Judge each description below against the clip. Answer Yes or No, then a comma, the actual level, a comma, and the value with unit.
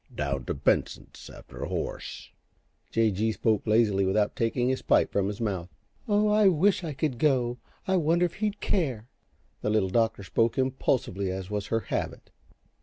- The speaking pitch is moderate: No, low, 115 Hz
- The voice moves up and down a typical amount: No, wide, 7.0 semitones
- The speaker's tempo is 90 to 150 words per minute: No, average, 175 wpm